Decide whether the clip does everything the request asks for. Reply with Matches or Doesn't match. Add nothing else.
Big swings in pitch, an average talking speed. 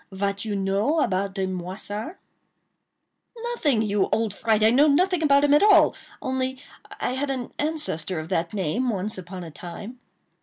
Matches